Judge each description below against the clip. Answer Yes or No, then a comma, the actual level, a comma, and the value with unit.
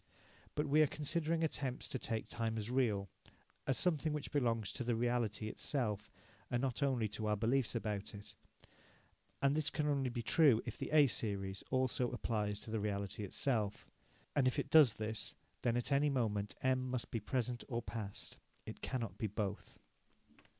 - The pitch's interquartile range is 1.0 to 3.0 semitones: No, average, 4.2 semitones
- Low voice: Yes, low, 120 Hz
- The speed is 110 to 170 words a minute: No, average, 180 wpm